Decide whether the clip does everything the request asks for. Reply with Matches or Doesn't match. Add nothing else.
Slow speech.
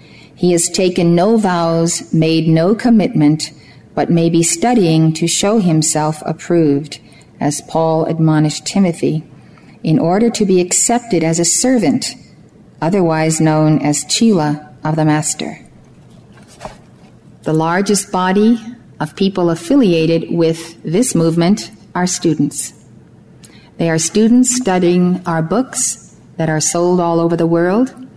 Matches